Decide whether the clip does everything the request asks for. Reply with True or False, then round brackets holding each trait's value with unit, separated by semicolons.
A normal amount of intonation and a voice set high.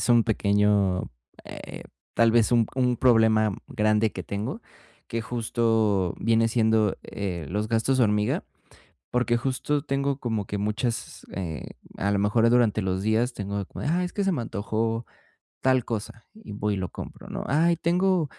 False (3.0 semitones; 110 Hz)